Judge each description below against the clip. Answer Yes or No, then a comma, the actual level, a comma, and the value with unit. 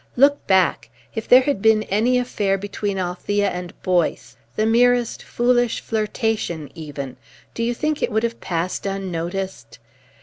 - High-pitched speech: Yes, high, 205 Hz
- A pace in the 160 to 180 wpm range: No, average, 145 wpm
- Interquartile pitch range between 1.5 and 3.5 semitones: No, average, 4.6 semitones